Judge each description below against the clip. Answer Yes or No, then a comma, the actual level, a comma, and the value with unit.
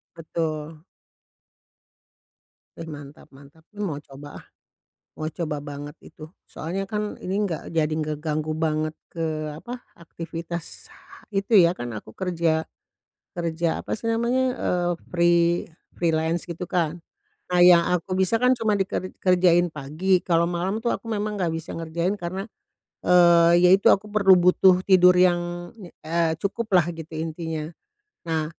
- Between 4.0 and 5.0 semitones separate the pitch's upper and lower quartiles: No, average, 2.8 semitones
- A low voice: No, medium, 170 Hz